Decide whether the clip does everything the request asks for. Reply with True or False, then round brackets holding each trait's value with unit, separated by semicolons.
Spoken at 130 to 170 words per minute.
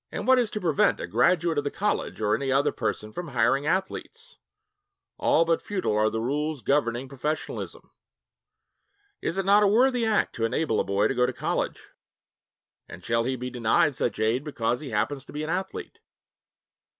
False (185 wpm)